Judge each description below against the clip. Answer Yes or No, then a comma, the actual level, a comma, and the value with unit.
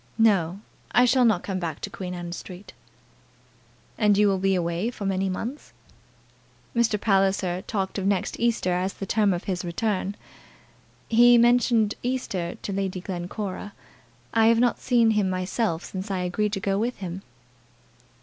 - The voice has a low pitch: No, high, 195 Hz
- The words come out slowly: No, average, 160 wpm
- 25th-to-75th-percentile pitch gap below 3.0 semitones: No, average, 3.3 semitones